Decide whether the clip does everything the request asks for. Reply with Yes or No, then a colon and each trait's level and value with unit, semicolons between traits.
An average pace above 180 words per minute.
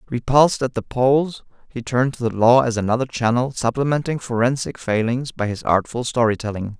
No: average, 175 wpm